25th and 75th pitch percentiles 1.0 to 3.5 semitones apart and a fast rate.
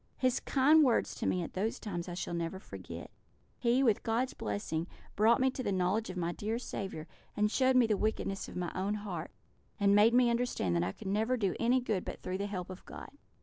No: average, 4.5 semitones; fast, 230 wpm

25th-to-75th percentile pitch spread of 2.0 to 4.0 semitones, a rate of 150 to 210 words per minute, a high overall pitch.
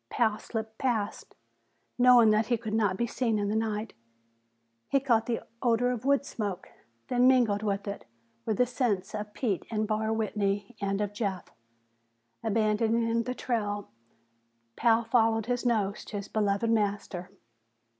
Yes: narrow, 2.4 semitones; average, 155 wpm; high, 220 Hz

